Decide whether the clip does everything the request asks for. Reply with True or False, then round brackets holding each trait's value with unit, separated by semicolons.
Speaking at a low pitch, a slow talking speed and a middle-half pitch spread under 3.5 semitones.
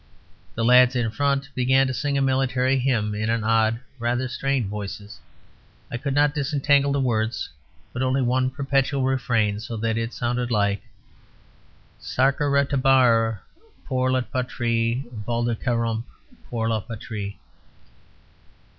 True (125 Hz; 125 wpm; 2.9 semitones)